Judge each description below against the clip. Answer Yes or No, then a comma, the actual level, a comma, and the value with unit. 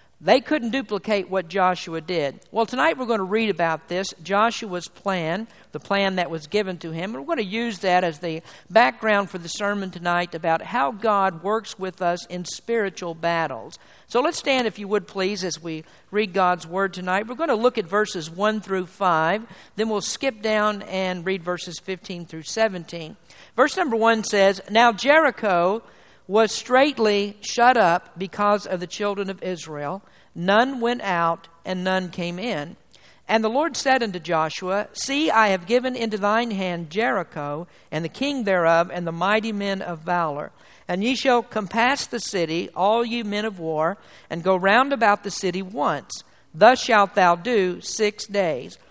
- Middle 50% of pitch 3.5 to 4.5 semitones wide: Yes, average, 3.9 semitones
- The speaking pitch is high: Yes, high, 195 Hz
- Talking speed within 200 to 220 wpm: No, average, 180 wpm